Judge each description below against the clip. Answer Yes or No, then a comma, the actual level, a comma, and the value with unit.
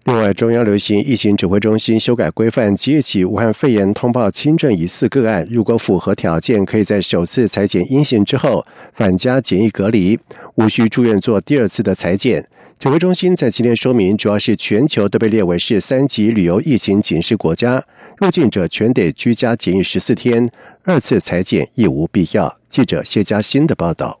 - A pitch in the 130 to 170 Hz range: No, low, 110 Hz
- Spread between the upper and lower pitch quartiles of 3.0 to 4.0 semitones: Yes, average, 3.4 semitones